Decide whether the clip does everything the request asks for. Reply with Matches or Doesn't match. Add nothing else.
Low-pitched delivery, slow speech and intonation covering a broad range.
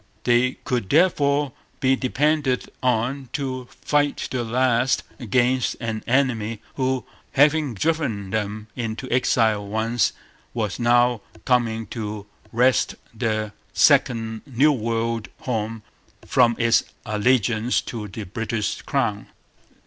Doesn't match